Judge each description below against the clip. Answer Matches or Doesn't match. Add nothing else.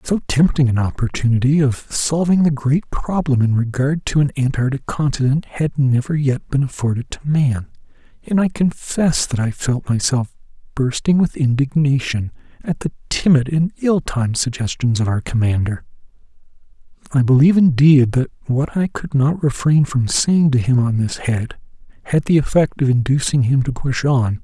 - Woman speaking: Doesn't match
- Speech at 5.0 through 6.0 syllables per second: Doesn't match